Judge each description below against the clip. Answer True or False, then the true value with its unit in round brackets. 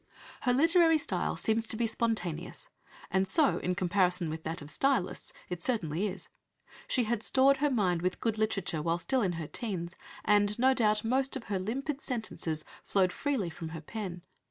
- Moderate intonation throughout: False (6.0 semitones)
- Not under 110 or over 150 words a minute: False (180 wpm)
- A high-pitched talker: True (210 Hz)